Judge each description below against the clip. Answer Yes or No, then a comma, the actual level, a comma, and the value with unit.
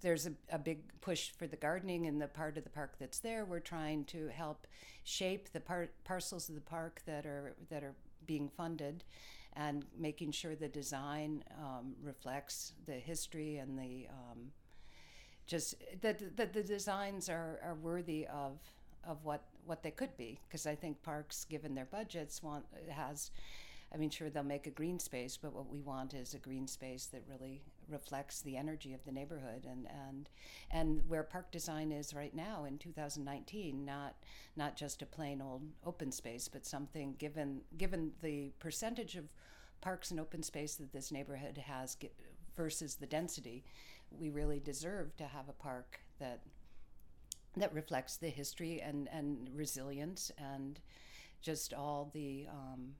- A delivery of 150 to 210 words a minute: Yes, average, 170 wpm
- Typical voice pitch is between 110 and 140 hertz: No, medium, 150 Hz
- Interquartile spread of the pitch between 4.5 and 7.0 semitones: No, average, 2.8 semitones